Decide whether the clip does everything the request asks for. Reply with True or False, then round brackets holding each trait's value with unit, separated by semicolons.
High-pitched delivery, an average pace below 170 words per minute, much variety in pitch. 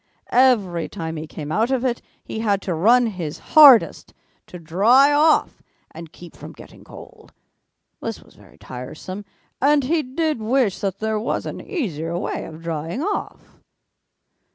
True (215 Hz; 155 wpm; 7.7 semitones)